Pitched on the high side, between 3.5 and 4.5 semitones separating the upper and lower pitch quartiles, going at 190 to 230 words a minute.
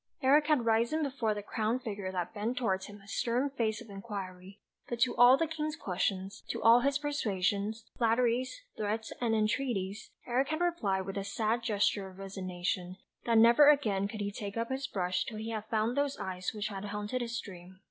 Yes: high, 220 Hz; average, 3.9 semitones; average, 200 wpm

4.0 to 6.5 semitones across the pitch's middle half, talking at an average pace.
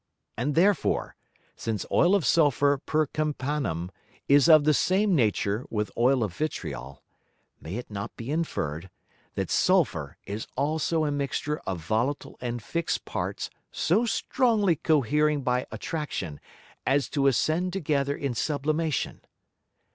No: average, 5.2 semitones; slow, 130 wpm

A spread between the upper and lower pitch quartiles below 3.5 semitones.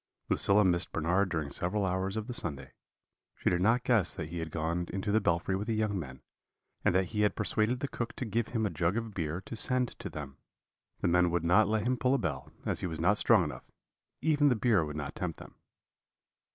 No: average, 4.7 semitones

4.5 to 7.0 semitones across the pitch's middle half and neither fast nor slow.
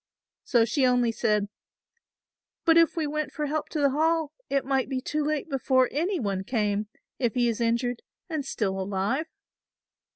Yes: average, 4.8 semitones; average, 170 wpm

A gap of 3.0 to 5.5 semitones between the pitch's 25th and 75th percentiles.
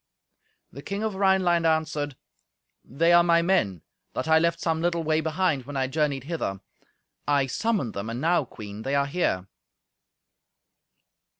Yes: average, 4.2 semitones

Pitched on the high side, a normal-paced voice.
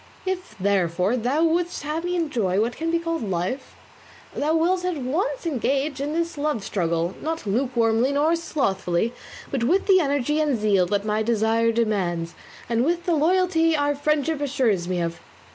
Yes: very high, 275 Hz; average, 170 wpm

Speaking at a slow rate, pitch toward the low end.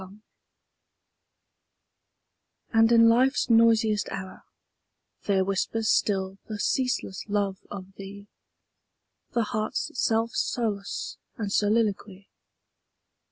No: slow, 95 wpm; high, 210 Hz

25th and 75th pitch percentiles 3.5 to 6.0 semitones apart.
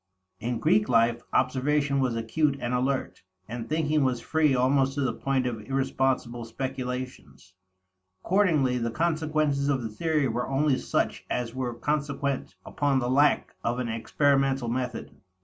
No: average, 2.9 semitones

